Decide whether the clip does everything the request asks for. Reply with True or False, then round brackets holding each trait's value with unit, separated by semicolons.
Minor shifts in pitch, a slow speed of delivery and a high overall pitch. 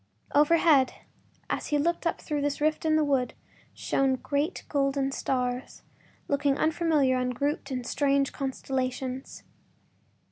True (2.2 semitones; 130 wpm; 280 Hz)